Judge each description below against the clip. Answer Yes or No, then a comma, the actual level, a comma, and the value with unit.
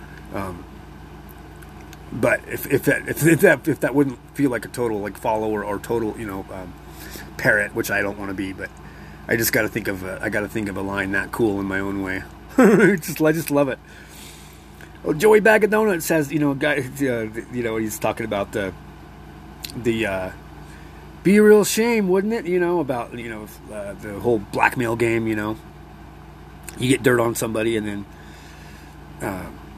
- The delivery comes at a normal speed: Yes, average, 190 wpm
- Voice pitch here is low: Yes, low, 110 Hz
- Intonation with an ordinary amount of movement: No, wide, 7.0 semitones